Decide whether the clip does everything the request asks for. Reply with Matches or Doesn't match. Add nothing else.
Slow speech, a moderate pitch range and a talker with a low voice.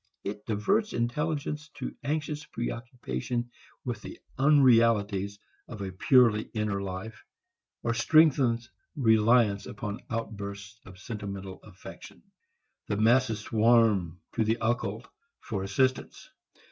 Matches